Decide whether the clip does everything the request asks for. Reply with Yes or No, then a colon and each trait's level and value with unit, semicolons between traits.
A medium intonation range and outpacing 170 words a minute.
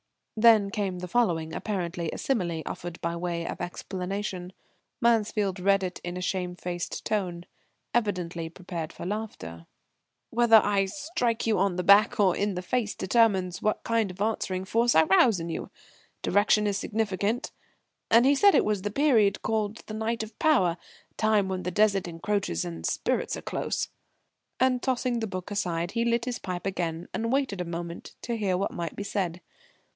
Yes: average, 3.9 semitones; average, 180 wpm